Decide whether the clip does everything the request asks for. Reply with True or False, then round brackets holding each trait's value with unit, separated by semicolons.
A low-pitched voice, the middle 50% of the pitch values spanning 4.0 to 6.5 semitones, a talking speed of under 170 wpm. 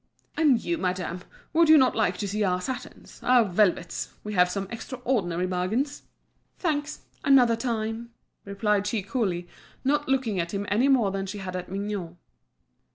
False (210 Hz; 5.6 semitones; 160 wpm)